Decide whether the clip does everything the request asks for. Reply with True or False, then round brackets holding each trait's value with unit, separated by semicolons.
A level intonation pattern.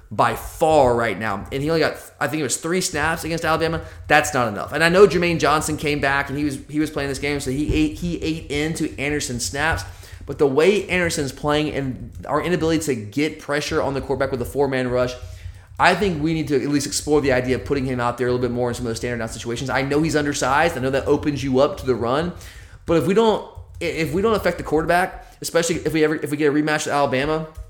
False (3.9 semitones)